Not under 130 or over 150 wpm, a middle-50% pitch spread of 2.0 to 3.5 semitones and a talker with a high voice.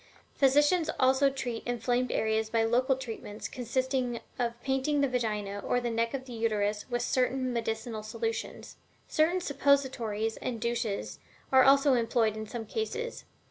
Yes: average, 140 wpm; average, 3.1 semitones; high, 245 Hz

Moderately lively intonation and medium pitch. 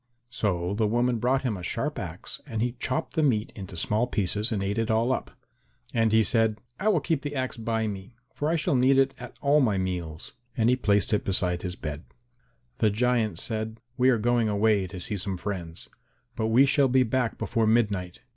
No: average, 3.8 semitones; low, 110 Hz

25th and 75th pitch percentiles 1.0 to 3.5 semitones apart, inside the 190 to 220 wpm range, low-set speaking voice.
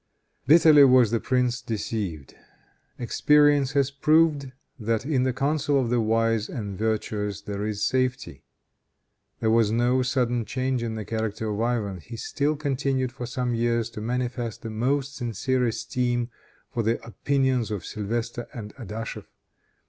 No: average, 2.8 semitones; average, 150 wpm; low, 120 Hz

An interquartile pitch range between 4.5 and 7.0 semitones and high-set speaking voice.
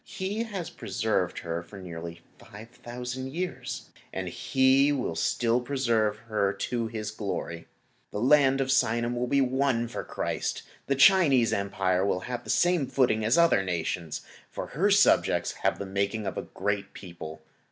No: average, 5.1 semitones; low, 115 Hz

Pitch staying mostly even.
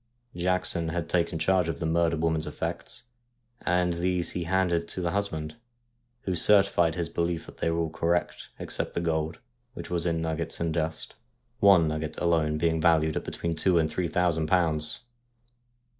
Yes: narrow, 1.6 semitones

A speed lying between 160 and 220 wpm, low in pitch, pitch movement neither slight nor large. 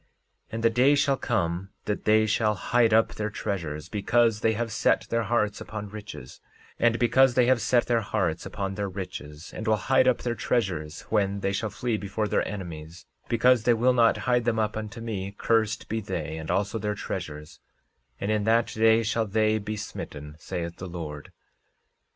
Yes: average, 190 wpm; low, 110 Hz; average, 3.0 semitones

